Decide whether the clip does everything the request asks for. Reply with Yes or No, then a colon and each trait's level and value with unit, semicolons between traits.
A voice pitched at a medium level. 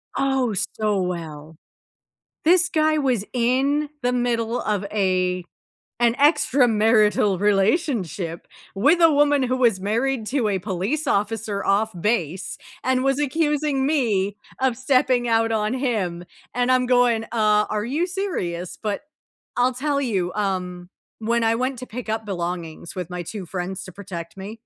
No: high, 225 Hz